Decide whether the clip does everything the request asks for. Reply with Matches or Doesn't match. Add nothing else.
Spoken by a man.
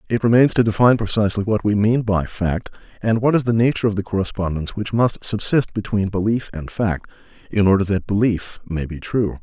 Matches